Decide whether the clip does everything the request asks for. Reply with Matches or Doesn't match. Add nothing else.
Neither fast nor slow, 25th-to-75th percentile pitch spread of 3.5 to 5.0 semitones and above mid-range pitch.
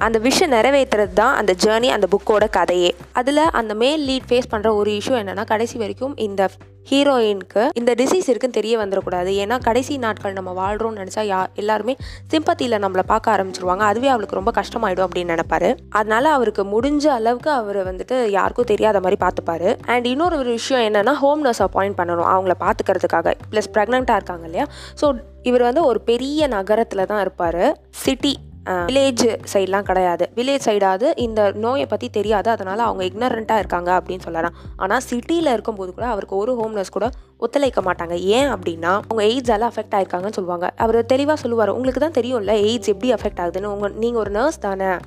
Doesn't match